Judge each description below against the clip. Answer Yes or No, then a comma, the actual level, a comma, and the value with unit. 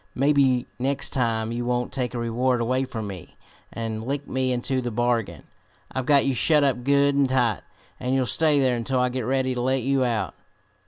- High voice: No, low, 125 Hz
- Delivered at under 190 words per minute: No, fast, 205 wpm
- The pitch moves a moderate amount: No, narrow, 2.0 semitones